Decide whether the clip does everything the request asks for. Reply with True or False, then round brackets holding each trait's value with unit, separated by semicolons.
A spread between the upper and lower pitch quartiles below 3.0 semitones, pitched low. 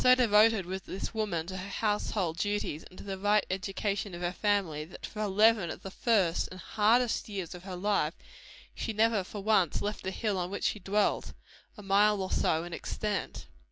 False (2.5 semitones; 200 Hz)